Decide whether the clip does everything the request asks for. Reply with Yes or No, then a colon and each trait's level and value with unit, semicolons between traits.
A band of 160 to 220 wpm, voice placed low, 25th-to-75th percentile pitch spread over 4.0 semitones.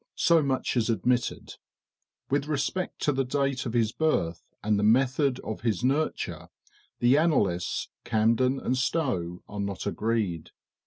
No: average, 145 wpm; low, 125 Hz; average, 4.4 semitones